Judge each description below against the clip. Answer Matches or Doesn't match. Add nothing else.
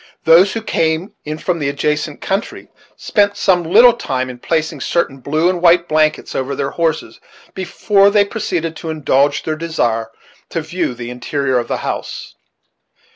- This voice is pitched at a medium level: Matches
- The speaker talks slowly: Doesn't match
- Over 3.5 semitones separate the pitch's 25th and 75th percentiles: Matches